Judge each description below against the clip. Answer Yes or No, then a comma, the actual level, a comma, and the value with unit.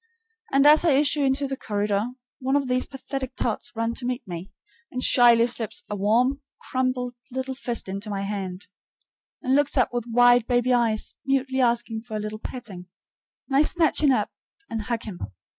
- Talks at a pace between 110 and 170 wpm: No, average, 185 wpm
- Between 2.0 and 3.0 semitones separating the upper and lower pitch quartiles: No, average, 3.5 semitones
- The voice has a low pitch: No, high, 245 Hz